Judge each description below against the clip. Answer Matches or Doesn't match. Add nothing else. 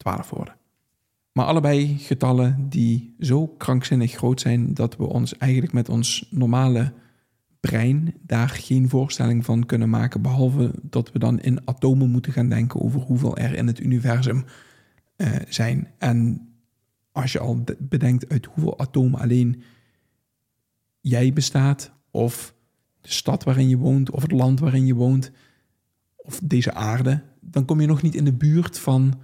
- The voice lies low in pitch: Matches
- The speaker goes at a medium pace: Matches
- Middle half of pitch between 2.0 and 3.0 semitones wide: Matches